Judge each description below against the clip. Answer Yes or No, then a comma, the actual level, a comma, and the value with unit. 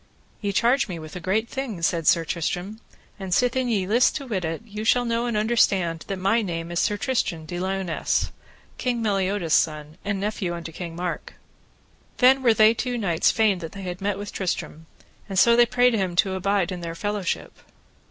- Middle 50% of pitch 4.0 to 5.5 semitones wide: Yes, average, 4.7 semitones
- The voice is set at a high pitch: Yes, high, 195 Hz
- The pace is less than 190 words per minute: No, average, 200 wpm